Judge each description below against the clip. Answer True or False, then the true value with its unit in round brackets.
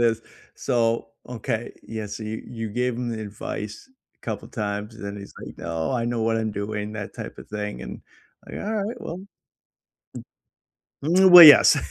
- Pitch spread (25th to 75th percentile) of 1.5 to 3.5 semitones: True (2.9 semitones)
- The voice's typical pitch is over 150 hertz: False (110 Hz)